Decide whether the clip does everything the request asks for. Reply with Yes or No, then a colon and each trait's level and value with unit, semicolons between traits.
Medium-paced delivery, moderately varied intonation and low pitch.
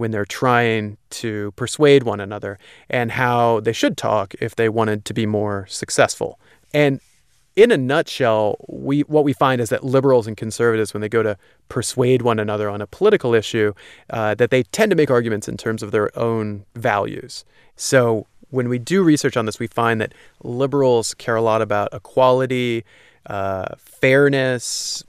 Yes: average, 175 wpm; average, 3.1 semitones; low, 115 Hz